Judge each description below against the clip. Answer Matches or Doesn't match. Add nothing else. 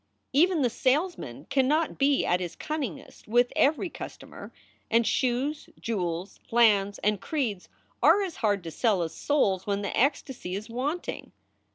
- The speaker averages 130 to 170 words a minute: Matches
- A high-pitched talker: Matches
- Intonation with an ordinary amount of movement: Doesn't match